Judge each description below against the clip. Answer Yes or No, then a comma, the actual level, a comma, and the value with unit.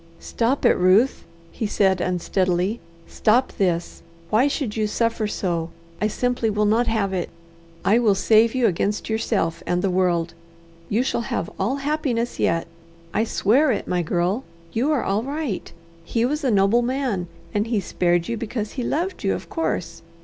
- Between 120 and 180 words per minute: Yes, average, 170 wpm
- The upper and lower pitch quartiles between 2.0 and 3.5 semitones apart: No, average, 4.7 semitones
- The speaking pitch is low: No, high, 215 Hz